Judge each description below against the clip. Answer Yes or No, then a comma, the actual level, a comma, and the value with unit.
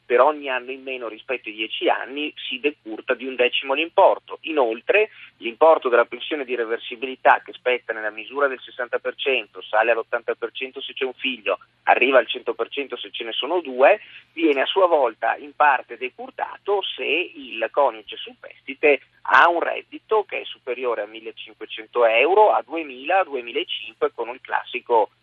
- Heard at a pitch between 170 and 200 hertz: Yes, medium, 185 Hz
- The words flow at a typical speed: Yes, average, 160 wpm